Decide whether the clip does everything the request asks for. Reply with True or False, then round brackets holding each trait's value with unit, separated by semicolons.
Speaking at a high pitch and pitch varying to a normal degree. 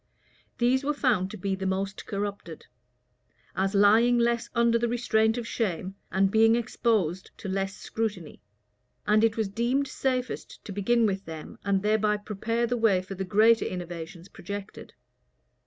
True (210 Hz; 3.4 semitones)